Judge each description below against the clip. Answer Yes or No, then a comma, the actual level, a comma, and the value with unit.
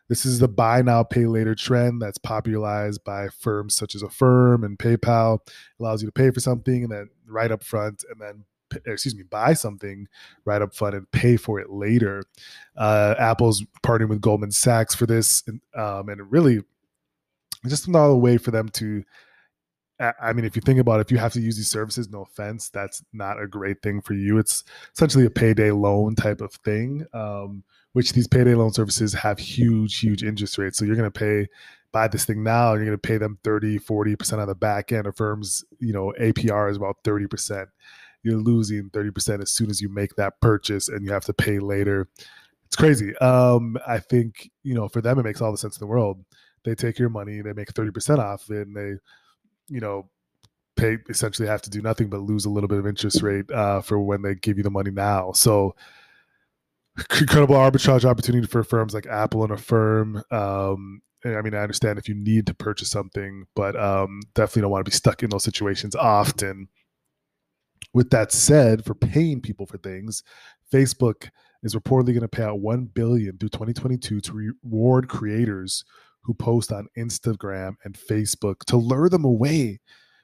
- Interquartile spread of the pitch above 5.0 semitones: No, narrow, 2.5 semitones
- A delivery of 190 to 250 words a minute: Yes, average, 200 wpm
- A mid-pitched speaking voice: No, low, 110 Hz